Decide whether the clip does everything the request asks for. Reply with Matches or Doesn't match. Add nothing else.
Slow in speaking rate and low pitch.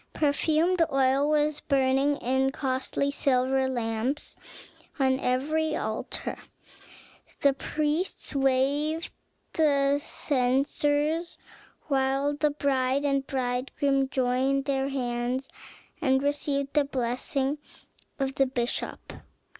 Doesn't match